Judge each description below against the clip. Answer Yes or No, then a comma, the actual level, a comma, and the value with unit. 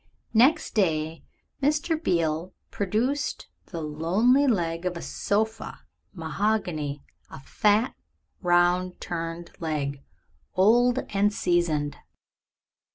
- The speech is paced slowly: Yes, slow, 95 wpm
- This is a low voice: No, medium, 180 Hz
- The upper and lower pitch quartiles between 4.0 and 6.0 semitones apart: Yes, average, 5.1 semitones